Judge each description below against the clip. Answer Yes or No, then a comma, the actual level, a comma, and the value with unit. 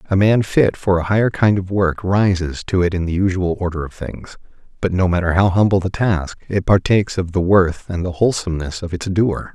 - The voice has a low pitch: Yes, very low, 95 Hz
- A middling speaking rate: No, fast, 220 wpm